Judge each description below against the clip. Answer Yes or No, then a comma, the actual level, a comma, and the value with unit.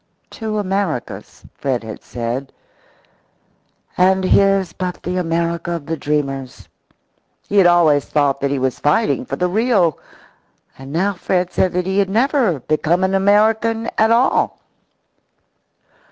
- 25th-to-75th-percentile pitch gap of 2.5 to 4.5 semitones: No, average, 5.3 semitones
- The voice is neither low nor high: Yes, medium, 180 Hz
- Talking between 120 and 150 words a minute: Yes, average, 140 wpm